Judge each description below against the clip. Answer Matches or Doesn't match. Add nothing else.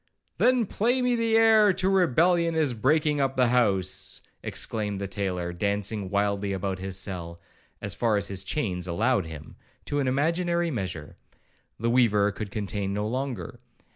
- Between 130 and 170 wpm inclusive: Matches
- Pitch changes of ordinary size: Doesn't match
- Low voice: Matches